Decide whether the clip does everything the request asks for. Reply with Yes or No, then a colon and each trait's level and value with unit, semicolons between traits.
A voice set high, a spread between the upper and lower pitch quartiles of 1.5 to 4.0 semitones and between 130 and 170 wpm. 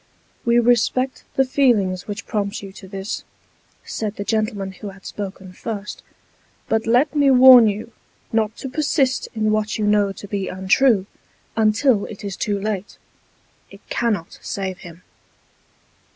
Yes: high, 215 Hz; average, 3.2 semitones; average, 150 wpm